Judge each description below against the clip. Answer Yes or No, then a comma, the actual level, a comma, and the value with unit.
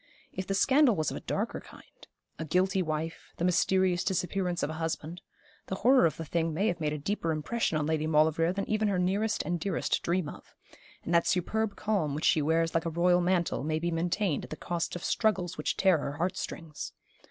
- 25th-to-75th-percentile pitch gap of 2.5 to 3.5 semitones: Yes, average, 3.0 semitones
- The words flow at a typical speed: No, fast, 220 wpm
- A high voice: No, medium, 175 Hz